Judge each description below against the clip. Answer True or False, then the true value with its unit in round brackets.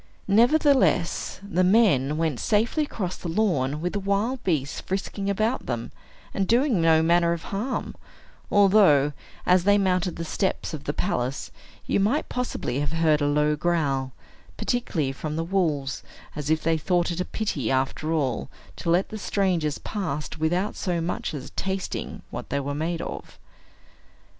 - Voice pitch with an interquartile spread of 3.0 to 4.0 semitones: False (5.0 semitones)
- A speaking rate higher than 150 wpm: True (160 wpm)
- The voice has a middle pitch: True (170 Hz)